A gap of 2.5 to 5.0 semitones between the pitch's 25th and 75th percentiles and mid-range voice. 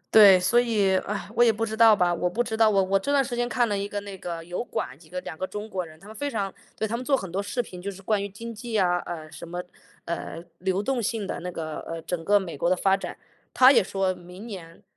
No: average, 3.8 semitones; high, 195 Hz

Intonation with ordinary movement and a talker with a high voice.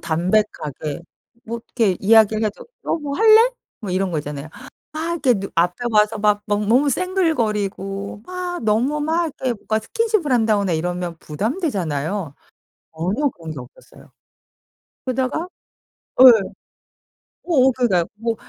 No: wide, 7.3 semitones; high, 215 Hz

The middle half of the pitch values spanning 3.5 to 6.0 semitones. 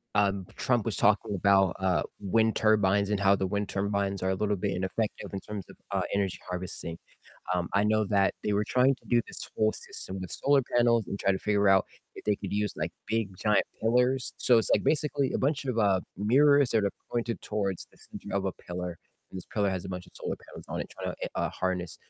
No: average, 2.9 semitones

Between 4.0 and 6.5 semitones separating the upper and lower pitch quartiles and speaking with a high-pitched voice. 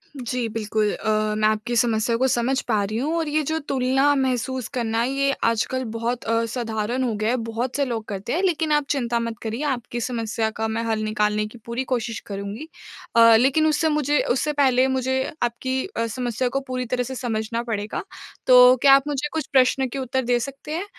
No: average, 2.9 semitones; high, 245 Hz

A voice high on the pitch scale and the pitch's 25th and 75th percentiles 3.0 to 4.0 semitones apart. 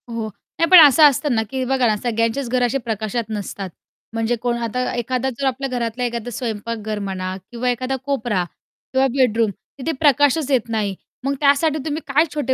Yes: high, 245 Hz; average, 3.3 semitones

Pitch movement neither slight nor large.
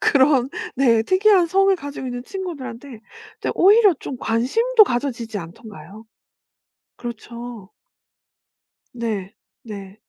No: wide, 7.3 semitones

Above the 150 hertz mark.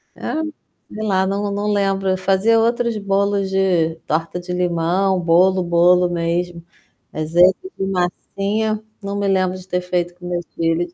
Yes: medium, 185 Hz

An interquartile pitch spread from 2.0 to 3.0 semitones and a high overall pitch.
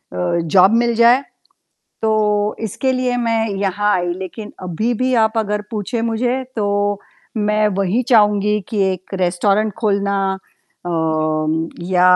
No: average, 3.7 semitones; high, 210 Hz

